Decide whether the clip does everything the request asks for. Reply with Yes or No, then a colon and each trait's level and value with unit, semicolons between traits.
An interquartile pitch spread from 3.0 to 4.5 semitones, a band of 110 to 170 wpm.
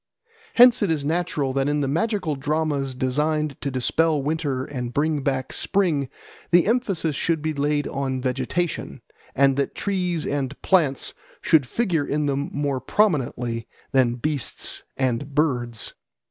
Yes: average, 3.3 semitones; average, 145 wpm